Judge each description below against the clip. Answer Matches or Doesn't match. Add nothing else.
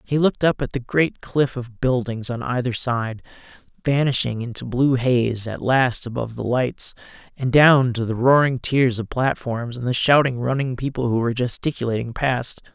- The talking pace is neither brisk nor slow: Matches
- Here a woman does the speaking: Doesn't match